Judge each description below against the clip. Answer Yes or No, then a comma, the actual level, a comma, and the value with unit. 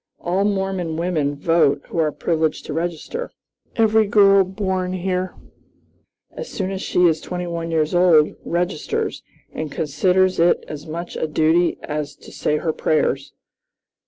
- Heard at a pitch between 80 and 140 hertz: No, medium, 170 Hz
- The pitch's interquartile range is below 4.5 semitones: Yes, average, 3.1 semitones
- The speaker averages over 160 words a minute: No, average, 150 wpm